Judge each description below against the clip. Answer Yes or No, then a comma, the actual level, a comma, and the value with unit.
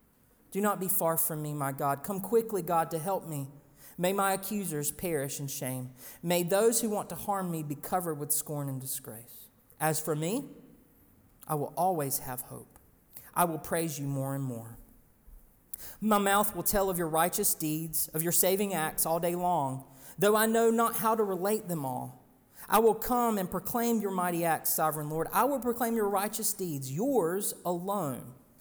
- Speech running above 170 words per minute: Yes, average, 190 wpm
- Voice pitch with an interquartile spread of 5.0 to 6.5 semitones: Yes, wide, 5.5 semitones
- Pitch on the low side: No, medium, 170 Hz